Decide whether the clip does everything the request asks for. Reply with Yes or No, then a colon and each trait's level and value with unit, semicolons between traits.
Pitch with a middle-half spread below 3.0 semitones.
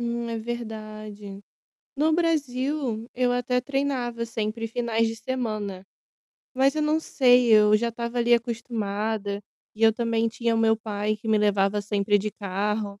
Yes: narrow, 2.5 semitones